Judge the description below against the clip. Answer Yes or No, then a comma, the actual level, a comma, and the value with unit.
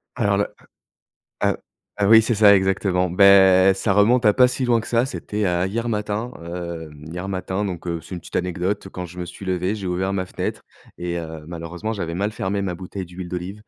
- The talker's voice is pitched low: Yes, very low, 95 Hz